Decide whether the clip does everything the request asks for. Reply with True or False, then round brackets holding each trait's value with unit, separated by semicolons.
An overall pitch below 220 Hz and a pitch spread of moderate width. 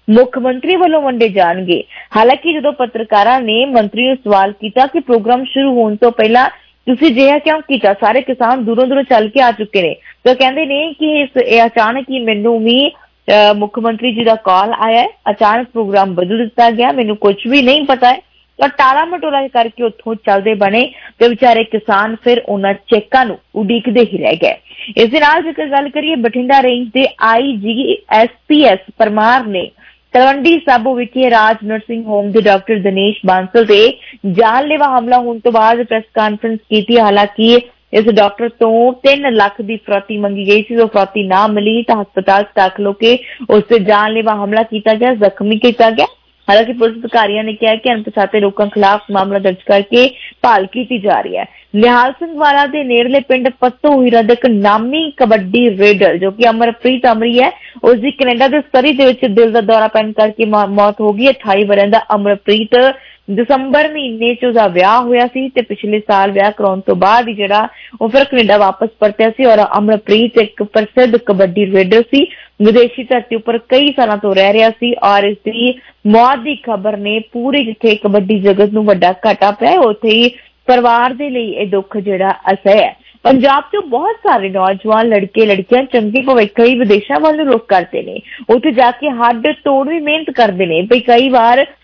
False (230 Hz; 3.4 semitones)